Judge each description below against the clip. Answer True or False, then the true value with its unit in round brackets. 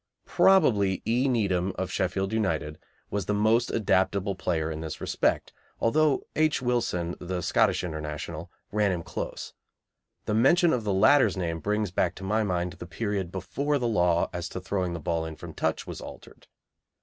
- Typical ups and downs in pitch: True (4.3 semitones)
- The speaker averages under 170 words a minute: False (175 wpm)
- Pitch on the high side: False (95 Hz)